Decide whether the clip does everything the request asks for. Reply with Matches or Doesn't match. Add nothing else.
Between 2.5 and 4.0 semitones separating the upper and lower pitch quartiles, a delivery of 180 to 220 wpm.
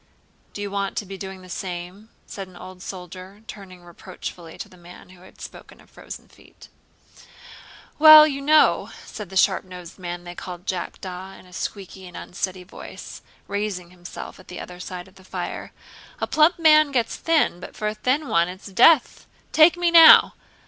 Matches